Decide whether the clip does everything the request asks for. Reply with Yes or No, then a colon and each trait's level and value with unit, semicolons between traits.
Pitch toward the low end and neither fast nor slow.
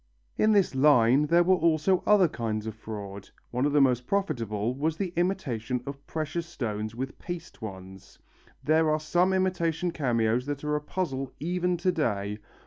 No: medium, 145 Hz; average, 170 wpm